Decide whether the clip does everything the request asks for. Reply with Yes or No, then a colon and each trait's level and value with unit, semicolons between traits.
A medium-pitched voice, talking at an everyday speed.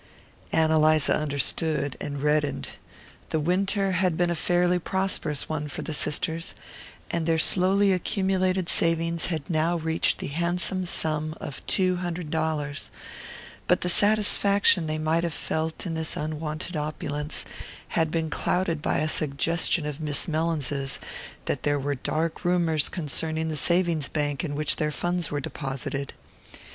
Yes: medium, 160 Hz; average, 150 wpm